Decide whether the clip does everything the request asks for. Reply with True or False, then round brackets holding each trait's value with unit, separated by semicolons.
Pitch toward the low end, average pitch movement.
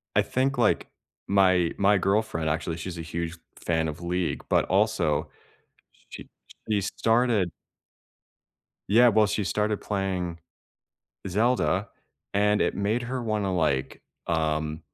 True (95 Hz; 4.3 semitones)